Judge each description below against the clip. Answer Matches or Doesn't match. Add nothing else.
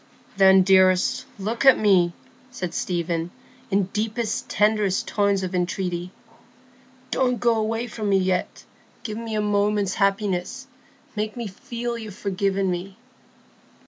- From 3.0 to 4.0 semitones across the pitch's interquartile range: Doesn't match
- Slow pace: Matches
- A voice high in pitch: Matches